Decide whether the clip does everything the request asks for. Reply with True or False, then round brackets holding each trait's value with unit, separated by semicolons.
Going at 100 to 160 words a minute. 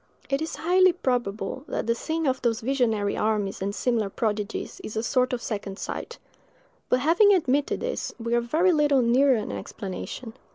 False (175 wpm)